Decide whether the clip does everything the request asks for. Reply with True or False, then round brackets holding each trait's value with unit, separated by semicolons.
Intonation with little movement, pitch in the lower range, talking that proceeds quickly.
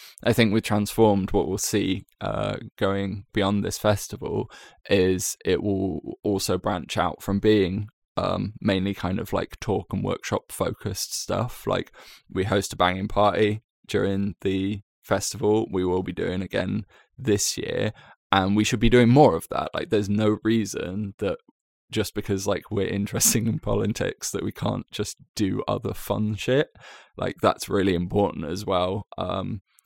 False (1.7 semitones; 100 Hz; 165 wpm)